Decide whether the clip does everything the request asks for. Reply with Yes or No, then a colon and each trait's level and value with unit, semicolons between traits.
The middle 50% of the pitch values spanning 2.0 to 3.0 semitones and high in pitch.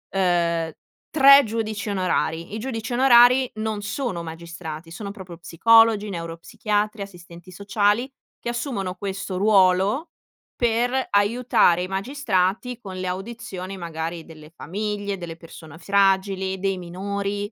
No: average, 3.8 semitones; high, 195 Hz